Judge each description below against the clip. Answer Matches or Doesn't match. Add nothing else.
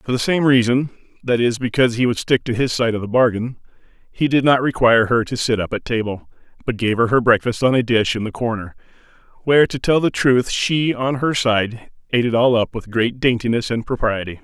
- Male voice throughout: Matches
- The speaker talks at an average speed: Doesn't match